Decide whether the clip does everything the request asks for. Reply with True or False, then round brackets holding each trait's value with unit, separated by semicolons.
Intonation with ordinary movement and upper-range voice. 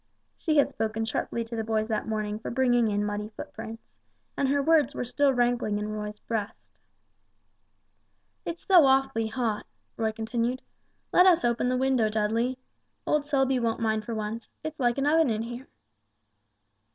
True (3.5 semitones; 235 Hz)